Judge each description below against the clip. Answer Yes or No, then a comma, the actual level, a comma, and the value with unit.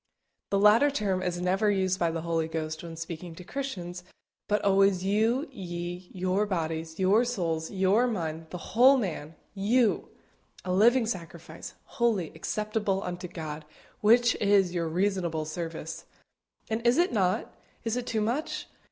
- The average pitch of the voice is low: No, high, 190 Hz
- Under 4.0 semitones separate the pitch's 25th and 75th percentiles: No, average, 4.3 semitones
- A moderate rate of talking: Yes, average, 150 wpm